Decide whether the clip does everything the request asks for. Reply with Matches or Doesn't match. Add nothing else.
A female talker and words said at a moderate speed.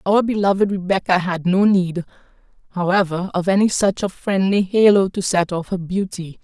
Matches